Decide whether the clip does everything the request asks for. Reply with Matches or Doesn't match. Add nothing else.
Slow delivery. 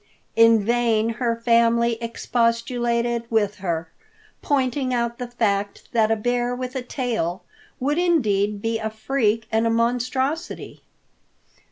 Matches